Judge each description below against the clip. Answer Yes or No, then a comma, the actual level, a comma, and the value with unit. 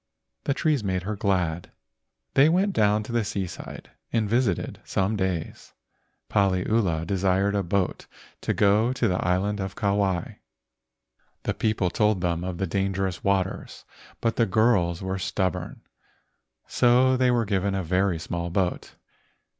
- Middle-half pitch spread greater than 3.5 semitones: No, average, 3.0 semitones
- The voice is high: No, low, 100 Hz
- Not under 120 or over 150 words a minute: Yes, average, 145 wpm